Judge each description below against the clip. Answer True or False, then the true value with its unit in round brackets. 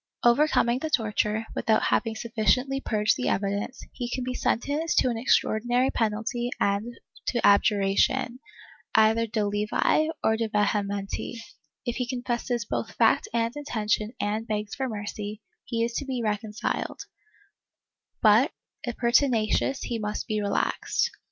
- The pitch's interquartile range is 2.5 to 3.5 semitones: True (2.8 semitones)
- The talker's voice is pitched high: True (225 Hz)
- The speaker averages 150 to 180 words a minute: False (140 wpm)